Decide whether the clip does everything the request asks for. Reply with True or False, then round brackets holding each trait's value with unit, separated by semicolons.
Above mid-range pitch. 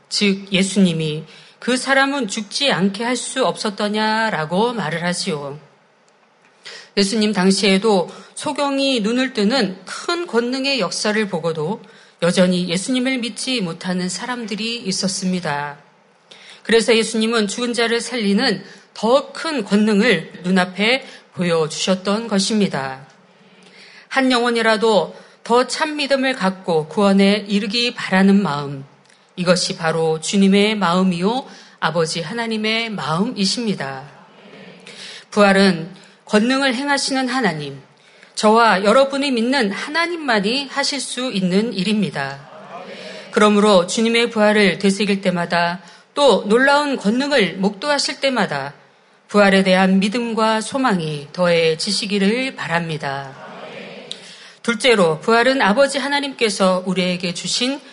True (210 Hz)